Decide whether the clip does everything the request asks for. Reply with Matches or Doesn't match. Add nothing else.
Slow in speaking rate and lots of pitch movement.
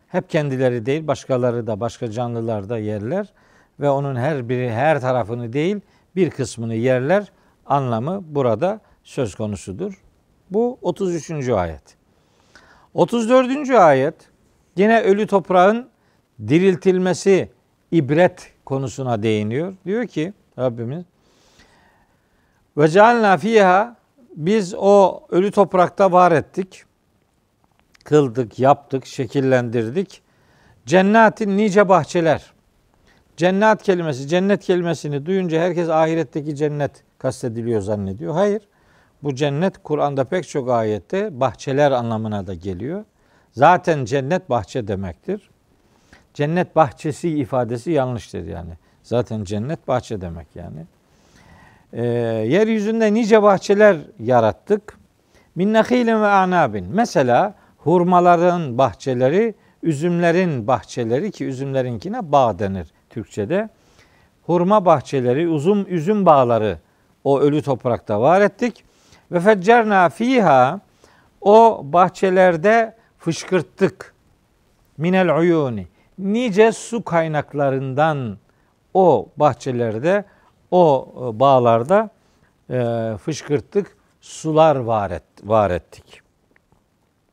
Matches